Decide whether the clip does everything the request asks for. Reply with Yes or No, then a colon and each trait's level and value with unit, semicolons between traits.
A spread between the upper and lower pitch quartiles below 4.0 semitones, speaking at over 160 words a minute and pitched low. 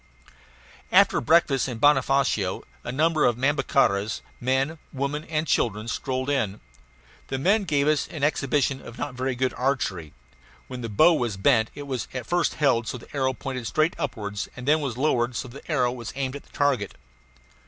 Yes: average, 3.3 semitones; average, 185 wpm; low, 130 Hz